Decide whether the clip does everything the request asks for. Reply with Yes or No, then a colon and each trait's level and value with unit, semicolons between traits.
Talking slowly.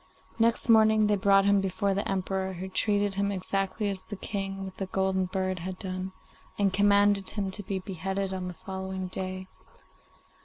No: average, 180 wpm